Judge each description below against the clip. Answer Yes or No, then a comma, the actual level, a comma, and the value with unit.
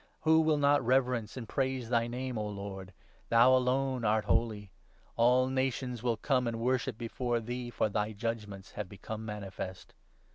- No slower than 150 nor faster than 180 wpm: Yes, average, 170 wpm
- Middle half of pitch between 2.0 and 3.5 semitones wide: Yes, average, 3.2 semitones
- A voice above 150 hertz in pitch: No, low, 120 Hz